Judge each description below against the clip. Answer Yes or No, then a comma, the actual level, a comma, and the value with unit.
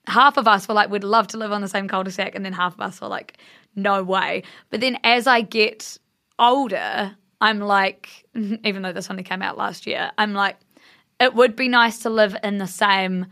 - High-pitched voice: Yes, high, 210 Hz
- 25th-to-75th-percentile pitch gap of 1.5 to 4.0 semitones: Yes, average, 2.9 semitones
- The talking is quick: Yes, fast, 230 wpm